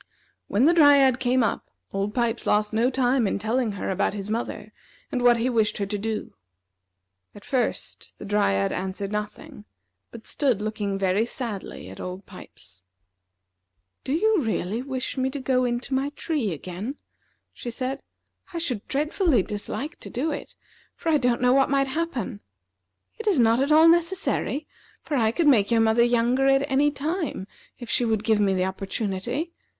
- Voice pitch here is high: Yes, high, 240 Hz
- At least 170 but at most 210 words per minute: Yes, average, 175 wpm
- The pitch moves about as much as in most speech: Yes, average, 4.7 semitones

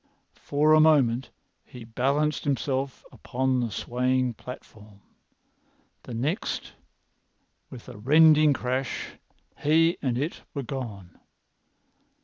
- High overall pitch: No, low, 130 Hz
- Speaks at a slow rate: Yes, slow, 105 wpm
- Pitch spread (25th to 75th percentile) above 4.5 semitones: No, average, 3.5 semitones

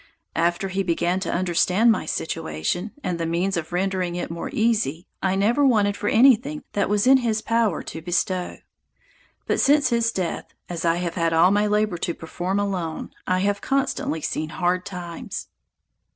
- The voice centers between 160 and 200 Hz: Yes, medium, 185 Hz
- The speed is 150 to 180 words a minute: Yes, average, 175 wpm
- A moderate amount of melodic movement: Yes, average, 3.7 semitones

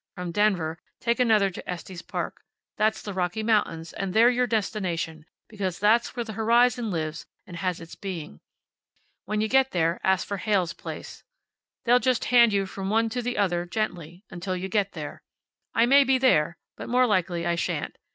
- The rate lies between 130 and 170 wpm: No, average, 185 wpm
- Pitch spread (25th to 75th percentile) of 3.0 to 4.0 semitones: No, average, 4.6 semitones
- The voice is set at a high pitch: Yes, high, 200 Hz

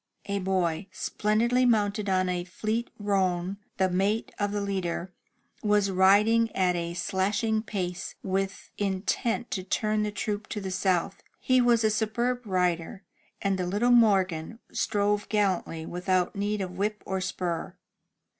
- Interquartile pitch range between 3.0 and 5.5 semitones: No, narrow, 2.4 semitones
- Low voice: No, high, 200 Hz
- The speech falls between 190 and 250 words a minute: No, average, 145 wpm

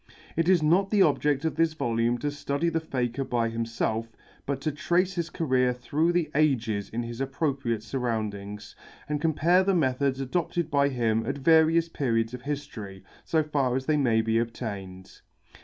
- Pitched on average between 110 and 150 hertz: Yes, low, 135 Hz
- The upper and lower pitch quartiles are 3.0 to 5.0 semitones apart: No, wide, 5.4 semitones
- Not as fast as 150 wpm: No, average, 175 wpm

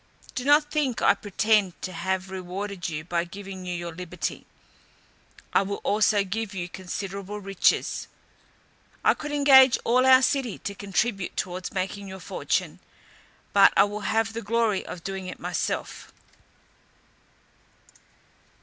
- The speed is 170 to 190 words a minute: No, average, 140 wpm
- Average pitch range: Yes, average, 3.3 semitones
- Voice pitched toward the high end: Yes, high, 200 Hz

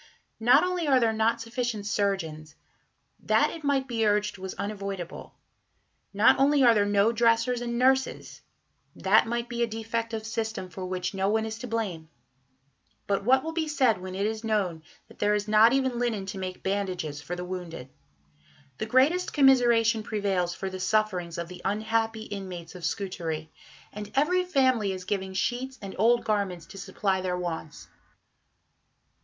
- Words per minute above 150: Yes, average, 170 wpm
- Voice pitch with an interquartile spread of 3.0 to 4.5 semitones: Yes, average, 4.0 semitones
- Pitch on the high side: Yes, high, 215 Hz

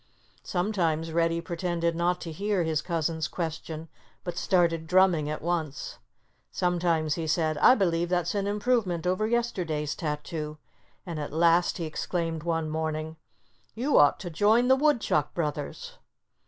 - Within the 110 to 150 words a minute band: Yes, average, 140 wpm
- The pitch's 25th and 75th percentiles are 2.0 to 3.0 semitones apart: Yes, narrow, 2.6 semitones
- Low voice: No, medium, 170 Hz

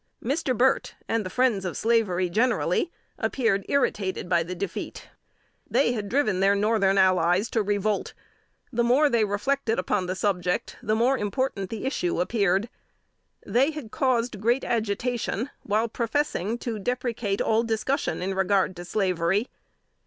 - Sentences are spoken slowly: No, average, 145 wpm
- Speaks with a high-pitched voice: Yes, high, 215 Hz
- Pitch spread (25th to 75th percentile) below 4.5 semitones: Yes, average, 4.0 semitones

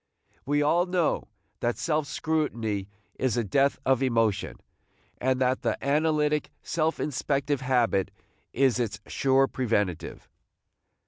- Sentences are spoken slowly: Yes, slow, 120 wpm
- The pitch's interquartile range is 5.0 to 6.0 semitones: No, average, 4.1 semitones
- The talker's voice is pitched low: Yes, low, 130 Hz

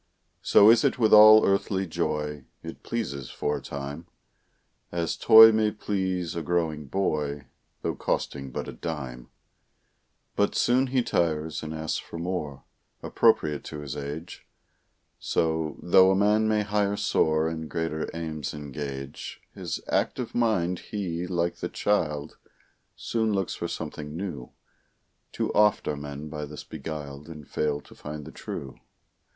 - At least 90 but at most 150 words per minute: Yes, average, 145 wpm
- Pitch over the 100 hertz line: No, very low, 80 Hz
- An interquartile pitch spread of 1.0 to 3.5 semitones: No, average, 4.9 semitones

